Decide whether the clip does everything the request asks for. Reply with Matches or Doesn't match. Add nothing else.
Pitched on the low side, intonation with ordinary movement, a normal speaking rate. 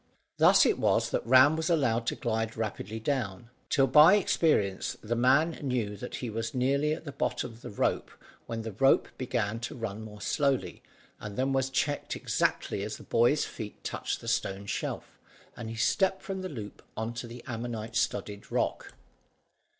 Matches